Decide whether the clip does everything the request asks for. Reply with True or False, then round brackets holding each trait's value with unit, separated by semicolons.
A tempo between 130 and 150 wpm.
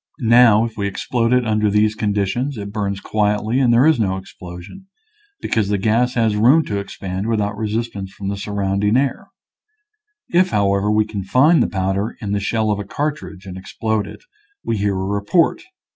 False (185 wpm)